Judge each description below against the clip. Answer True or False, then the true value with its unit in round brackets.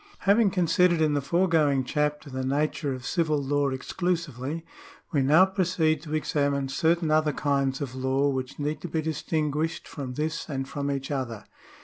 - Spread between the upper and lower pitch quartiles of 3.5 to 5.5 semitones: False (2.9 semitones)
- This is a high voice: False (150 Hz)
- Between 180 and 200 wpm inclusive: False (165 wpm)